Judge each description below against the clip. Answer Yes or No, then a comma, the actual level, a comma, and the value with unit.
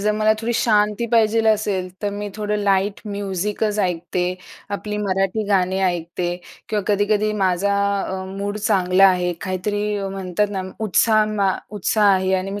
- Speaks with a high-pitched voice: Yes, high, 200 Hz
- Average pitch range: No, narrow, 1.9 semitones